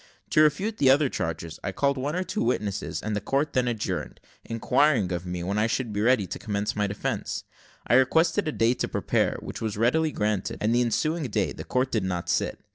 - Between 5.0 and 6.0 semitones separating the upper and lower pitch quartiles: Yes, wide, 5.4 semitones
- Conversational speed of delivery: No, fast, 220 wpm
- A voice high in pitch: No, low, 120 Hz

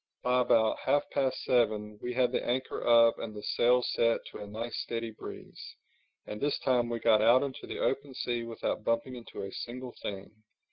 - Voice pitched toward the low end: Yes, low, 120 Hz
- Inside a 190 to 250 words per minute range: Yes, average, 195 wpm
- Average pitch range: No, narrow, 2.1 semitones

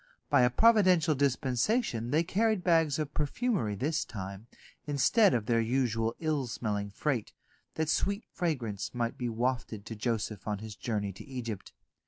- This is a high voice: No, low, 125 Hz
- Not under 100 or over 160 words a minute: Yes, average, 155 wpm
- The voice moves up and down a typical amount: No, wide, 6.1 semitones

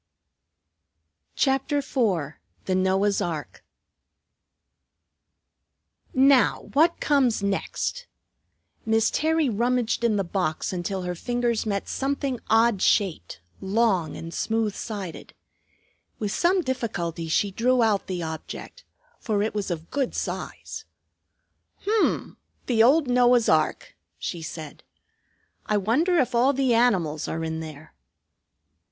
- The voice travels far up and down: Yes, wide, 5.7 semitones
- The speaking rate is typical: No, slow, 115 wpm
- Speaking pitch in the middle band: No, high, 220 Hz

